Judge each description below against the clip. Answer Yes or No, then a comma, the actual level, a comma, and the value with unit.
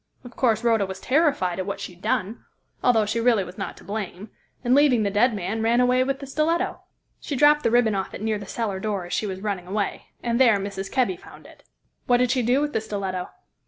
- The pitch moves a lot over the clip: No, average, 4.0 semitones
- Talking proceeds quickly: Yes, fast, 240 wpm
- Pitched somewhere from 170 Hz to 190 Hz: No, high, 220 Hz